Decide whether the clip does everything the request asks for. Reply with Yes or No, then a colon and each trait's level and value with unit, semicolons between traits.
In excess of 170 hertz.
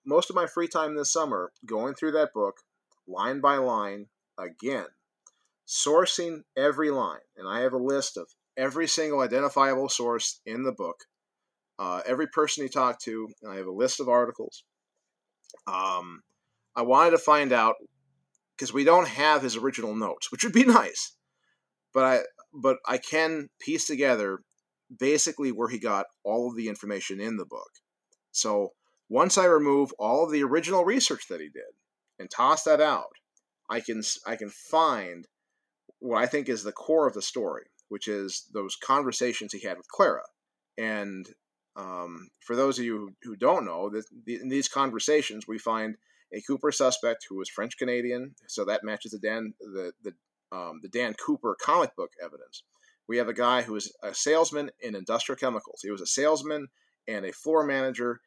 No: low, 135 Hz